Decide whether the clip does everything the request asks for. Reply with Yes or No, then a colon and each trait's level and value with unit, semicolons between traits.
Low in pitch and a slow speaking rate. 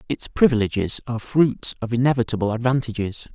Yes: low, 120 Hz; slow, 125 wpm